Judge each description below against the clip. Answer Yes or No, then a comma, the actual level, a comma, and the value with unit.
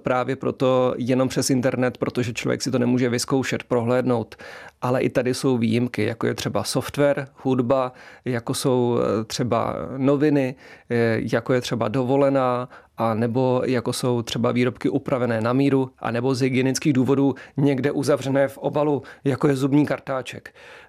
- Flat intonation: Yes, narrow, 1.9 semitones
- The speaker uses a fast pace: No, average, 150 wpm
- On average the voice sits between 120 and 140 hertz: Yes, low, 130 Hz